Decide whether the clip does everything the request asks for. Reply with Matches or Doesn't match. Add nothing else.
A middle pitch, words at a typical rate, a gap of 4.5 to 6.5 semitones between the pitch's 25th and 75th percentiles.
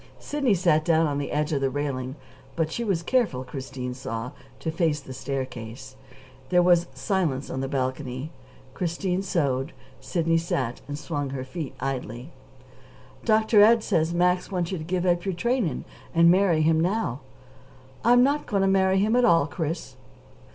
Matches